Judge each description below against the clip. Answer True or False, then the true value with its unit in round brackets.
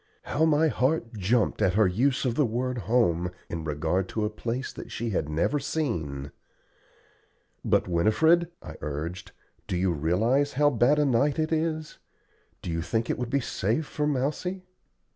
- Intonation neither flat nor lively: False (8.3 semitones)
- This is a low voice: True (120 Hz)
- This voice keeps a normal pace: True (170 wpm)